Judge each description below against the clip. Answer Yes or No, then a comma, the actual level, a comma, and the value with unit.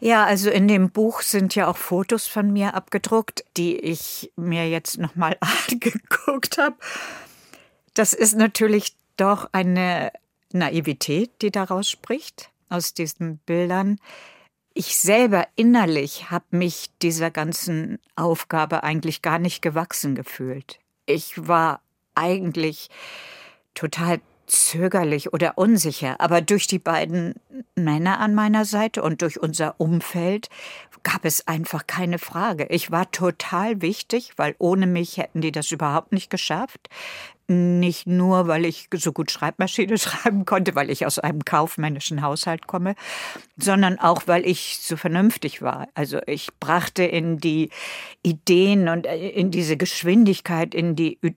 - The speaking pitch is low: No, medium, 175 Hz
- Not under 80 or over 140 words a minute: Yes, average, 135 wpm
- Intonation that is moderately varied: Yes, average, 3.5 semitones